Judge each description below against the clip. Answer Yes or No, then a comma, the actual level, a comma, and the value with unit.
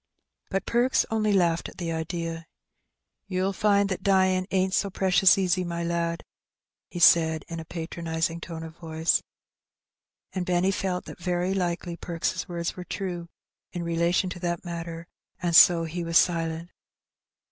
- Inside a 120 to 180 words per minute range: Yes, average, 160 wpm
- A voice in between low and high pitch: Yes, medium, 175 Hz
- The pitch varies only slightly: Yes, narrow, 1.9 semitones